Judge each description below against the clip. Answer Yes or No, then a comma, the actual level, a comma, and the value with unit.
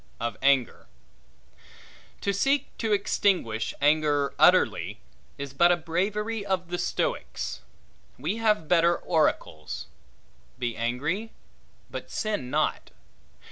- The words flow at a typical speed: No, slow, 105 wpm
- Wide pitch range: Yes, wide, 6.5 semitones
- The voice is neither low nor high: Yes, medium, 170 Hz